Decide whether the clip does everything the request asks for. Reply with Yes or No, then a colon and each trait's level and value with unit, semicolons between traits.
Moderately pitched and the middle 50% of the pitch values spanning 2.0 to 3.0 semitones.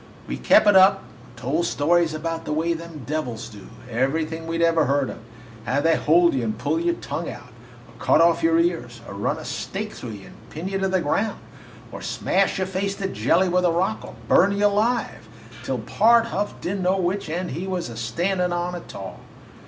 No: medium, 170 Hz; average, 4.8 semitones